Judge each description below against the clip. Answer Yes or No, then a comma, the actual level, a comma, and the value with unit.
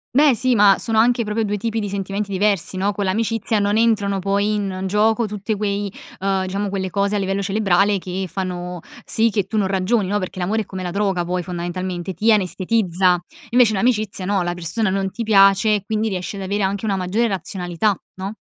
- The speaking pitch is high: Yes, high, 200 Hz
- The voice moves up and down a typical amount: No, narrow, 2.2 semitones